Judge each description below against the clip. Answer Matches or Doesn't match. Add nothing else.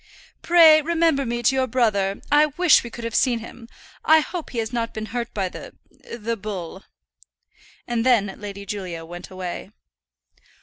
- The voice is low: Doesn't match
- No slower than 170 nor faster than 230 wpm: Matches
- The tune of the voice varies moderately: Matches